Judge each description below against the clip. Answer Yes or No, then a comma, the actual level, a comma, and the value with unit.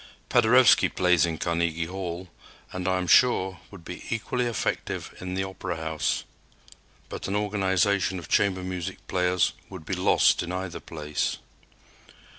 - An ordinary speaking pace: Yes, average, 145 wpm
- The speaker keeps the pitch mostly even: Yes, narrow, 2.1 semitones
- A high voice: No, very low, 90 Hz